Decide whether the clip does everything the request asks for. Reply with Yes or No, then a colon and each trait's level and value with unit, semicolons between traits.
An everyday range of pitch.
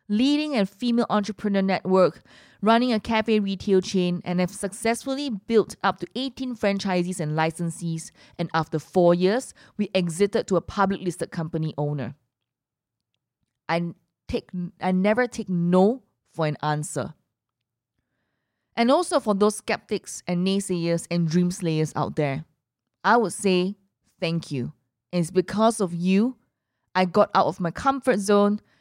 Yes: average, 4.7 semitones